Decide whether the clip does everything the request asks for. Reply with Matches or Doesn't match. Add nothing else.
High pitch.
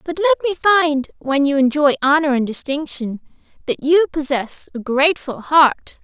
Matches